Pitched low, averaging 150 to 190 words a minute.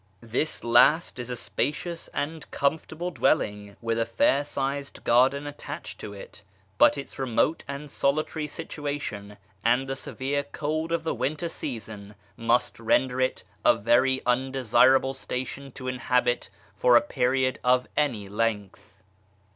No: low, 130 Hz; average, 140 wpm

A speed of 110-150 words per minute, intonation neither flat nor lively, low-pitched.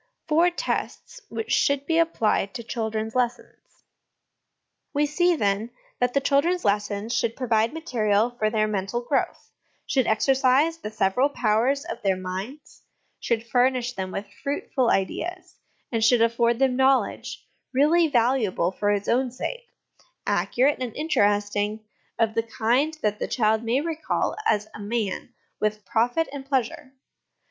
No: average, 145 wpm; average, 4.6 semitones; high, 240 Hz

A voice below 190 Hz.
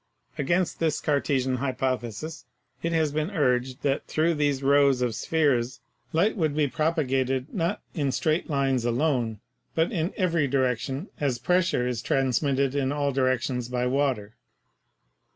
Yes: medium, 140 Hz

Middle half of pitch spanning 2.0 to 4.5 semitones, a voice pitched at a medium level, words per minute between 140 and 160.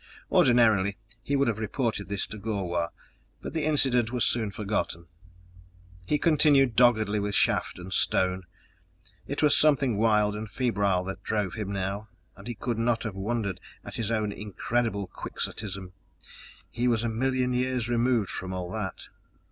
No: average, 3.4 semitones; low, 110 Hz; average, 155 wpm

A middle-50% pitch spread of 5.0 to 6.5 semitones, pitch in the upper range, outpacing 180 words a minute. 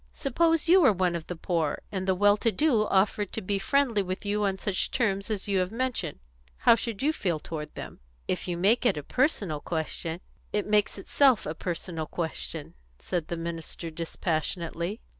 No: average, 4.5 semitones; high, 195 Hz; average, 195 wpm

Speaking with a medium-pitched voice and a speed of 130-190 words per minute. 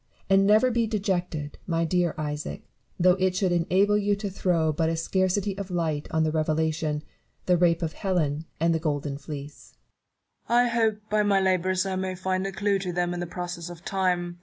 No: medium, 180 Hz; average, 200 wpm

